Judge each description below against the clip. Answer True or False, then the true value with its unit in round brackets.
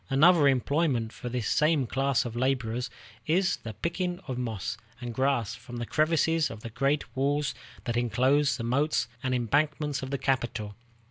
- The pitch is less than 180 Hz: True (135 Hz)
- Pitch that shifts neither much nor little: True (3.6 semitones)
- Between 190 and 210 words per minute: False (170 wpm)